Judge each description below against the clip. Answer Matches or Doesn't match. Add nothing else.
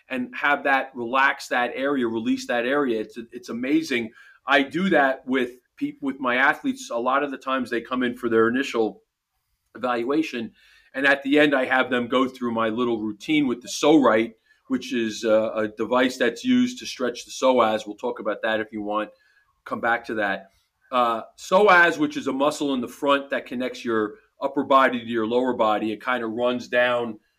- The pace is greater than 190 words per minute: Matches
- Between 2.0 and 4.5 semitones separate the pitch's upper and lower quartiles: Matches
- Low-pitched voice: Matches